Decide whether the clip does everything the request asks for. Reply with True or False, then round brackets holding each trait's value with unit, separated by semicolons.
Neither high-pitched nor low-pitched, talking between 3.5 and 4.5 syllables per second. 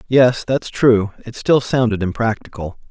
False (115 Hz; 4.4 syllables/s)